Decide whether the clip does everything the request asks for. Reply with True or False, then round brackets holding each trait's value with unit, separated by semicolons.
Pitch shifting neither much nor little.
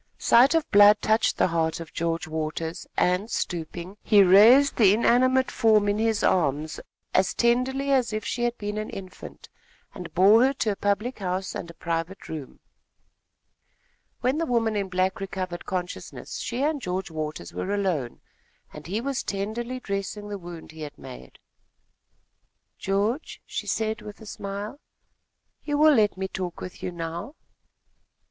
True (4.8 semitones)